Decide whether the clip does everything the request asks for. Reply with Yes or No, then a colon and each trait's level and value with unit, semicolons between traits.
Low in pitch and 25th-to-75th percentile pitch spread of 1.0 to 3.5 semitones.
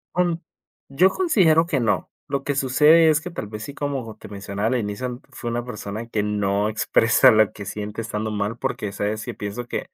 No: low, 115 Hz; average, 5.1 semitones